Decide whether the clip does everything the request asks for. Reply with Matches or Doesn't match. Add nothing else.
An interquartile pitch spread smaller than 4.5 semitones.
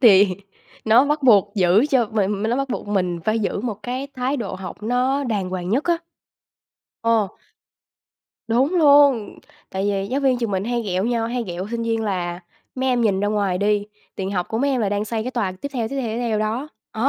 Matches